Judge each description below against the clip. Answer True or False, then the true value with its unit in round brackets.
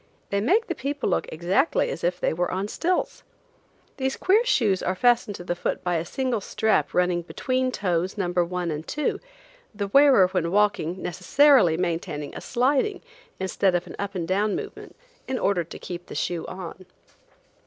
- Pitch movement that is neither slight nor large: False (6.6 semitones)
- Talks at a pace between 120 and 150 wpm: False (180 wpm)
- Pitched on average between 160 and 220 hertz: True (190 Hz)